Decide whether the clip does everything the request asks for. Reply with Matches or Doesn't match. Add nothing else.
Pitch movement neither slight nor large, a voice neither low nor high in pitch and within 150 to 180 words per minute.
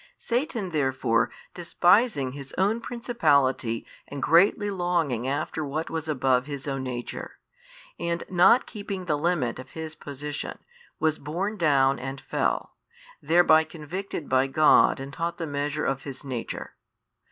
Doesn't match